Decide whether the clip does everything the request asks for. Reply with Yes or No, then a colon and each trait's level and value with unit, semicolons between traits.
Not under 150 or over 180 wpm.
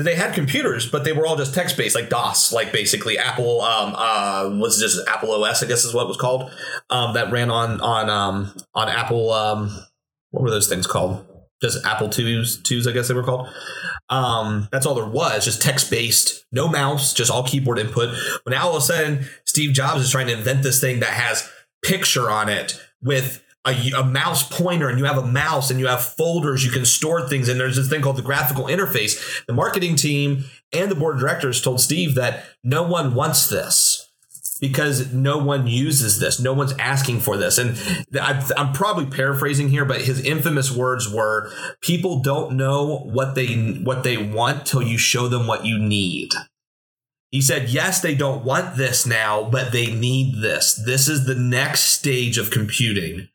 No: average, 200 wpm